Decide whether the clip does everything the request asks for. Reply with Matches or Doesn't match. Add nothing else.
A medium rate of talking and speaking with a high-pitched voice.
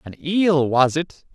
Doesn't match